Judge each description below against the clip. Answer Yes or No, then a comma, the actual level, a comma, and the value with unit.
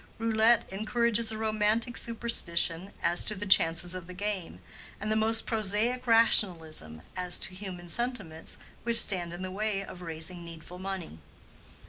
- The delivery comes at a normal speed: Yes, average, 150 wpm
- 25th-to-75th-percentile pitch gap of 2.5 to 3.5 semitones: No, average, 4.1 semitones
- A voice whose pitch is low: No, high, 195 Hz